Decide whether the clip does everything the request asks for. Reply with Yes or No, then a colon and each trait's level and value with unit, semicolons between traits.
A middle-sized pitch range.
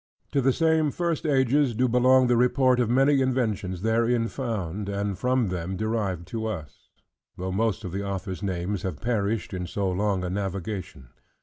Yes: average, 5.0 semitones